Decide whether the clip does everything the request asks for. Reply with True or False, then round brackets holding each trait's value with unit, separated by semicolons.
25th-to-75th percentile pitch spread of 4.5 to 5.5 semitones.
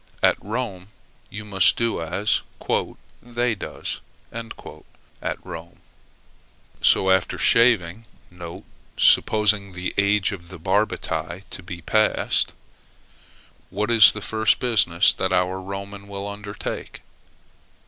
False (2.7 semitones)